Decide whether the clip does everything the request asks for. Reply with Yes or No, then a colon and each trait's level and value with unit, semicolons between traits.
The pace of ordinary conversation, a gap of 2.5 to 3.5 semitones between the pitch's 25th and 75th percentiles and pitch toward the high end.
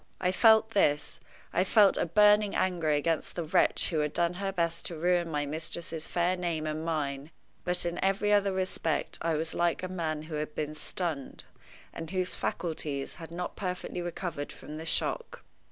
No: average, 185 wpm; average, 2.9 semitones; medium, 170 Hz